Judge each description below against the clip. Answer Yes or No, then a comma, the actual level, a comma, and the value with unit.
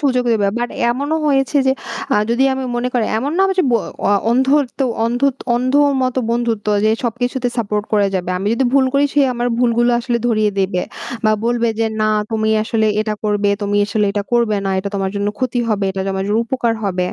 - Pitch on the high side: Yes, high, 235 Hz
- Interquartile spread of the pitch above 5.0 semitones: No, average, 3.5 semitones